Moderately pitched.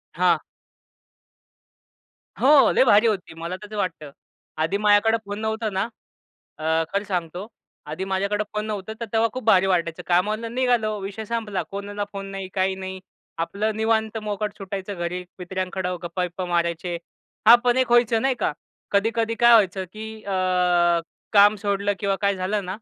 No: high, 200 Hz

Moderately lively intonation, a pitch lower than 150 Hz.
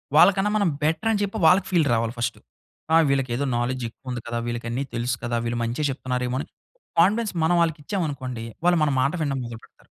No: wide, 6.0 semitones; low, 135 Hz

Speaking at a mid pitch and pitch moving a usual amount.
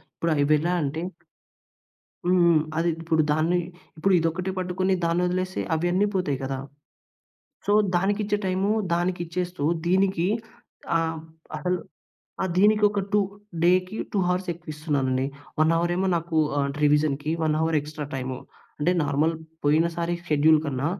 Yes: medium, 170 Hz; average, 3.2 semitones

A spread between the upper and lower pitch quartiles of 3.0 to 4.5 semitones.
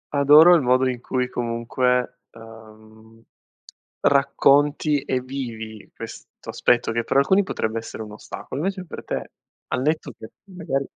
Yes: average, 4.1 semitones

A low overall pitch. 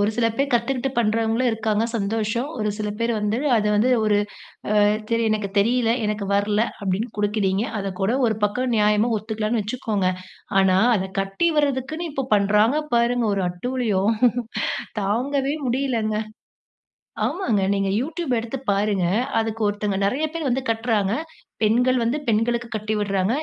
No: high, 220 Hz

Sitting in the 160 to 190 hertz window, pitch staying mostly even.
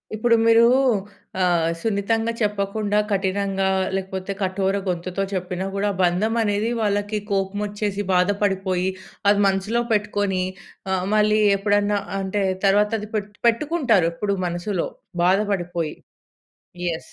No: high, 200 Hz; narrow, 1.7 semitones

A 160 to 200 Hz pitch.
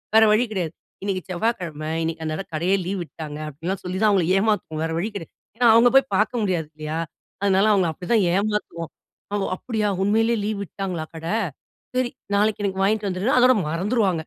Yes: high, 195 Hz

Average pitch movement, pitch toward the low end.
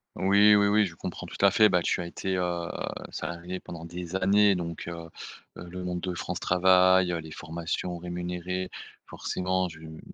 No: narrow, 1.5 semitones; very low, 90 Hz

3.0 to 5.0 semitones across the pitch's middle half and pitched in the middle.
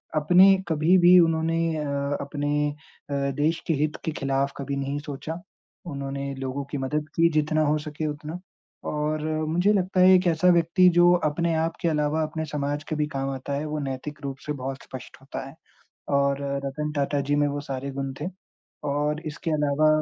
No: narrow, 2.5 semitones; medium, 150 Hz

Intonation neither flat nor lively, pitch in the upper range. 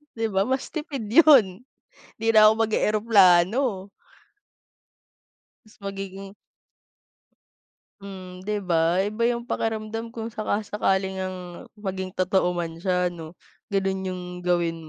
Yes: average, 3.0 semitones; high, 195 Hz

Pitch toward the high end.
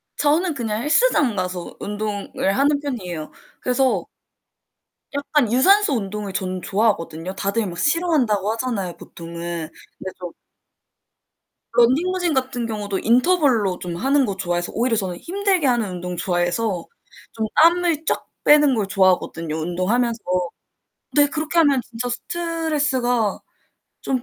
Yes: high, 230 Hz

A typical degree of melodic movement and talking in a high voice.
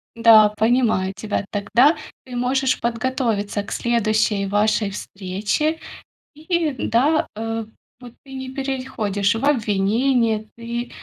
Yes: average, 3.7 semitones; high, 230 Hz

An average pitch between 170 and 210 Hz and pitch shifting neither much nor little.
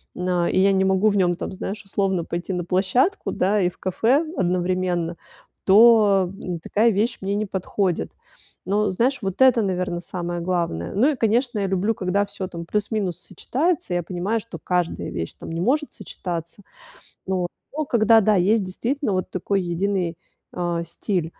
Yes: high, 190 Hz; average, 3.3 semitones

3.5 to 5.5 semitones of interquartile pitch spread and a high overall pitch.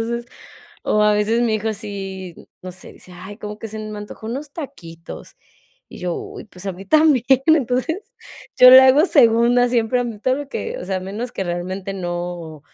Yes: average, 4.7 semitones; high, 215 Hz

